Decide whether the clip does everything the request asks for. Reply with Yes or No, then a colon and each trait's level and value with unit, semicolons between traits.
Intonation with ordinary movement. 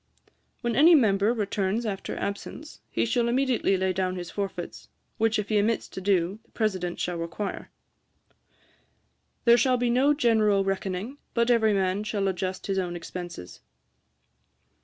Yes: average, 3.8 semitones